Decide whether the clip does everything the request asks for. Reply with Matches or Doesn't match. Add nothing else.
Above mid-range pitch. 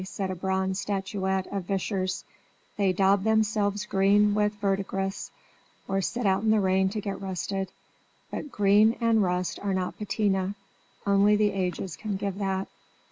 Matches